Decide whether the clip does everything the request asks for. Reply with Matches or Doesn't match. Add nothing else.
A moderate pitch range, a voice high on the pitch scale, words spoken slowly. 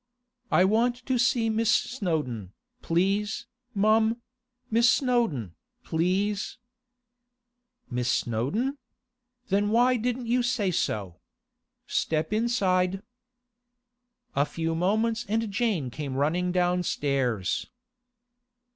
Doesn't match